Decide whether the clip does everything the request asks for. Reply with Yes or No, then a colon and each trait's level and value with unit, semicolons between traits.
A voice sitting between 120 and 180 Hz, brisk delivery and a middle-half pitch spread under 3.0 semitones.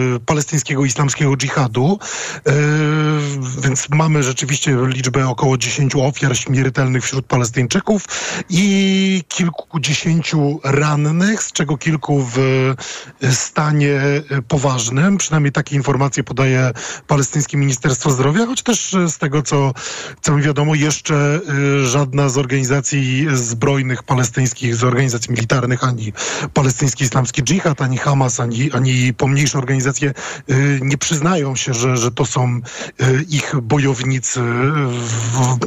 No: medium, 140 Hz; average, 115 wpm; narrow, 2.4 semitones